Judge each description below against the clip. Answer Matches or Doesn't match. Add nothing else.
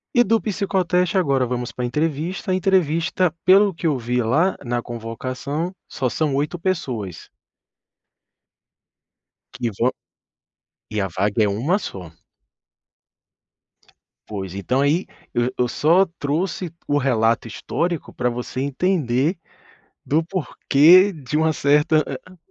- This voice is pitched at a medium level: Matches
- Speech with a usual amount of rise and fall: Doesn't match